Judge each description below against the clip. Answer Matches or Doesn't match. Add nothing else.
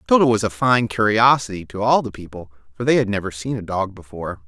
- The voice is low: Matches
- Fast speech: Matches